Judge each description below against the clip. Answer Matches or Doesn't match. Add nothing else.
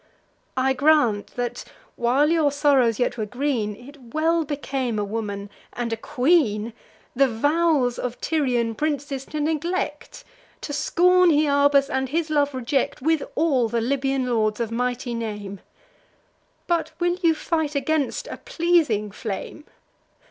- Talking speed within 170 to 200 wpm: Doesn't match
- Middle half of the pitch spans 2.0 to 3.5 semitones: Doesn't match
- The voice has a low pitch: Doesn't match